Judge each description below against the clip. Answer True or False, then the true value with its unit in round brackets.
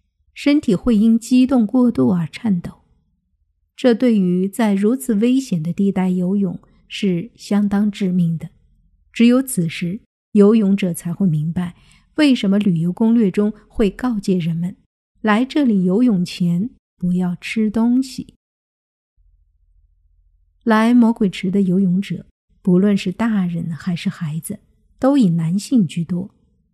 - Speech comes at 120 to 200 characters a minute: True (195 characters per minute)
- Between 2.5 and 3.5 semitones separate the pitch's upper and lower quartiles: False (4.5 semitones)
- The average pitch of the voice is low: False (195 Hz)